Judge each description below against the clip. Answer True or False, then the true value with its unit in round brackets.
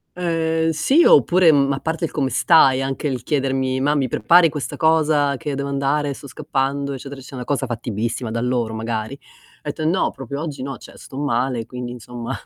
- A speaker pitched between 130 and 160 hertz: True (140 Hz)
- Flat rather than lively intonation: False (3.2 semitones)